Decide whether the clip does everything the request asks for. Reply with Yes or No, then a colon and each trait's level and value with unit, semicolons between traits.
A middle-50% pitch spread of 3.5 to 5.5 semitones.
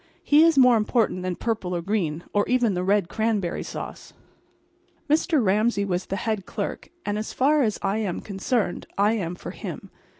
Yes: average, 4.0 semitones